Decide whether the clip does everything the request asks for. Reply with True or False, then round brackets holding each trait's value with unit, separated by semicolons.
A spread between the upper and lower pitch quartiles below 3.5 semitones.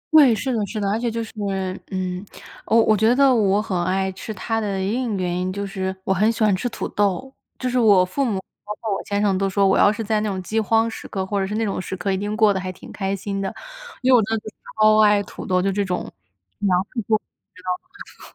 True (2.6 semitones)